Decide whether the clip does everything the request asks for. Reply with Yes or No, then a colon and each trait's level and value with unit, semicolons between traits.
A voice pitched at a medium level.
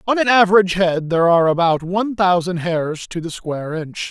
Yes: medium, 180 Hz